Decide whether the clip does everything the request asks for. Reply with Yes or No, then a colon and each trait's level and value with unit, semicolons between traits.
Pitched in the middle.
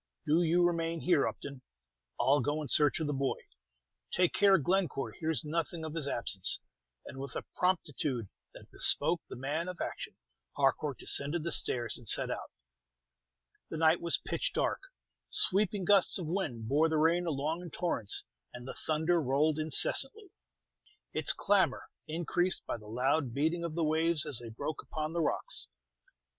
Yes: medium, 155 Hz